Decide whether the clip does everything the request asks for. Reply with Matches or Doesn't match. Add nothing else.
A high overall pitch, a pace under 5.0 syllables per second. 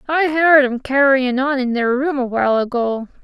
Matches